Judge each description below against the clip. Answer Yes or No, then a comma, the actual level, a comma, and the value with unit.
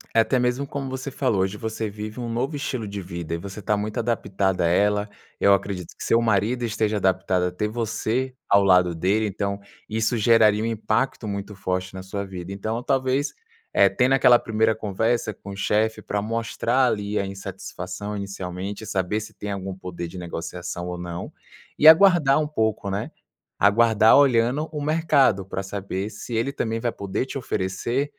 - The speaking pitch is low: Yes, low, 105 Hz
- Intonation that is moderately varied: Yes, average, 3.6 semitones